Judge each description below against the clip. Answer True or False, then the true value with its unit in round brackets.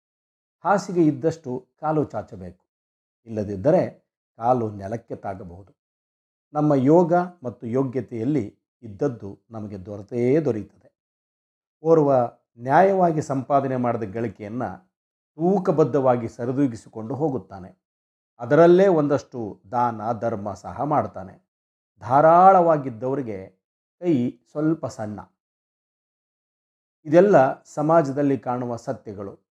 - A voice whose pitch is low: True (120 Hz)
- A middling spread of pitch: False (6.3 semitones)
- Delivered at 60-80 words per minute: True (75 wpm)